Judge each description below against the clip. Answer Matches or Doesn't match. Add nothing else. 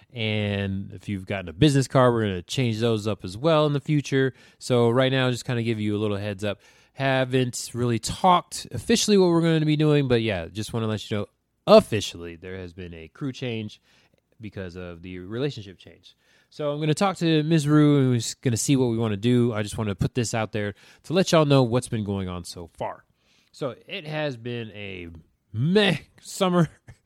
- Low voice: Matches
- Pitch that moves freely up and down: Matches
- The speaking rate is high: Matches